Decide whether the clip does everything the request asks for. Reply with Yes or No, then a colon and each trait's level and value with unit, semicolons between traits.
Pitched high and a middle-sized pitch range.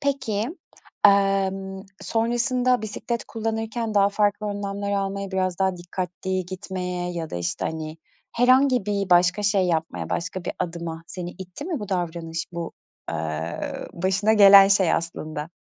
Yes: high, 195 Hz; average, 3.0 semitones